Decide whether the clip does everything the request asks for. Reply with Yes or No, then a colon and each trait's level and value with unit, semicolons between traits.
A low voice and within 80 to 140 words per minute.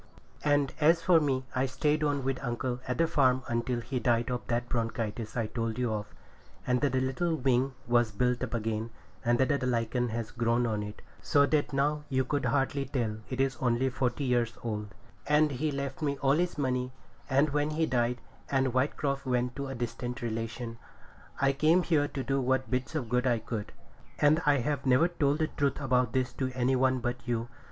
No: low, 130 Hz; average, 200 wpm